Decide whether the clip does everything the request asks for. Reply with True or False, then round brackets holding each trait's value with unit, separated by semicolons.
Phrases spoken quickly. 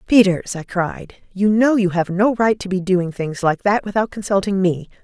True (215 wpm)